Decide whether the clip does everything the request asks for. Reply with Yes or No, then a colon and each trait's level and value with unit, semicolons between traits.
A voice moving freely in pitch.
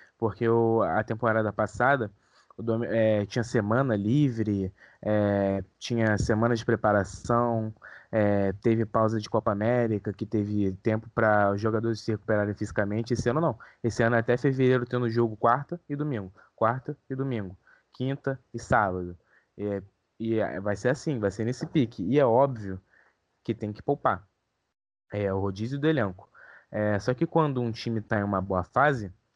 No: average, 2.8 semitones